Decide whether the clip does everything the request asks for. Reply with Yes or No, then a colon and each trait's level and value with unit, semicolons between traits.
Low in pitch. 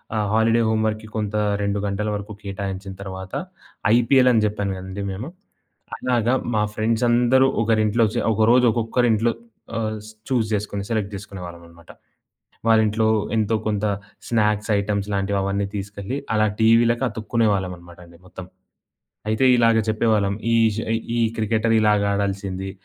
Yes: low, 110 Hz